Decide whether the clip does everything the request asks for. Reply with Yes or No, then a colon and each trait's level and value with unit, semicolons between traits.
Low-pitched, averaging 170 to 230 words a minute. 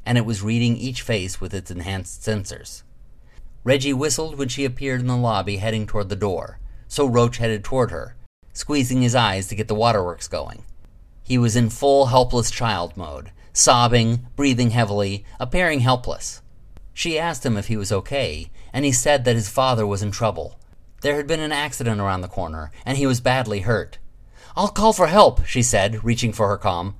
Yes: low, 115 Hz; average, 190 wpm